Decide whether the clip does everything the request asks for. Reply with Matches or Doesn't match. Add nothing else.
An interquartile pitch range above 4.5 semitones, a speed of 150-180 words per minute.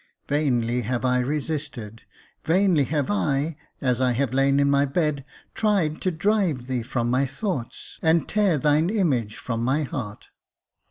Doesn't match